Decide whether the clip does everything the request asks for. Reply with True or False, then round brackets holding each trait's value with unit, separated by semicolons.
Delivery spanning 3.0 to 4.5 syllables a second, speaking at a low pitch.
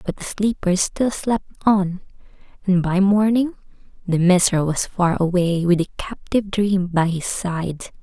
False (4.3 syllables/s; 190 Hz)